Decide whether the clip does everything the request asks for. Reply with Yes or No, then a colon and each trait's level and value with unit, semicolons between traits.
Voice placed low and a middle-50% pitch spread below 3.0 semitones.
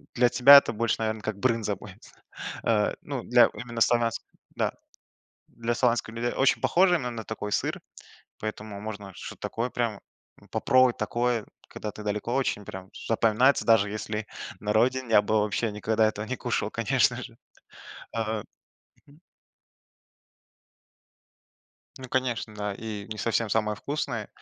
Yes: low, 110 Hz; narrow, 2.4 semitones